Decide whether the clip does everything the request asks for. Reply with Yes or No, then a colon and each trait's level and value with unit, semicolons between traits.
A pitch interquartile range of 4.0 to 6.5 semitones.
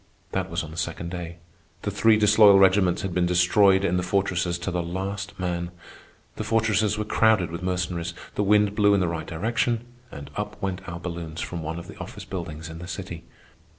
No: average, 2.9 semitones